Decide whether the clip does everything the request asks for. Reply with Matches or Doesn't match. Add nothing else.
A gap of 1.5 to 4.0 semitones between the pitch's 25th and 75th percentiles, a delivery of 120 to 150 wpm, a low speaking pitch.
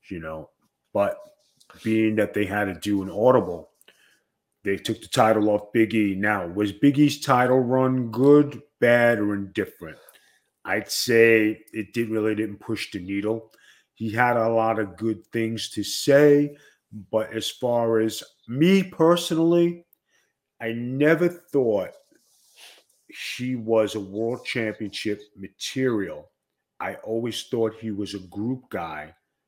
Matches